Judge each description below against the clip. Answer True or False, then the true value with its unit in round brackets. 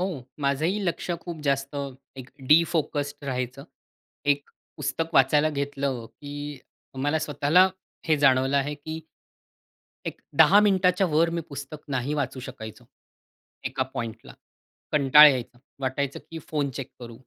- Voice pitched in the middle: True (145 Hz)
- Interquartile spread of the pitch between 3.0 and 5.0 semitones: False (2.6 semitones)